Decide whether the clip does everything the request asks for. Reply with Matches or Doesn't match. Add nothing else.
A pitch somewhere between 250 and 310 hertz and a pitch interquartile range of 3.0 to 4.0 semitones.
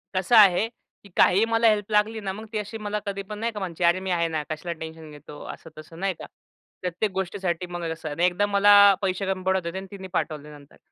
Doesn't match